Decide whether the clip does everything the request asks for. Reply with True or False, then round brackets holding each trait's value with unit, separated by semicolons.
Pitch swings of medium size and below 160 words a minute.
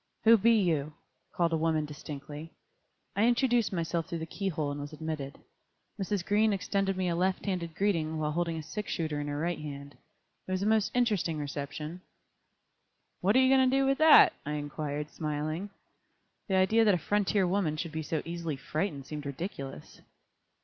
False (4.8 semitones; 185 wpm)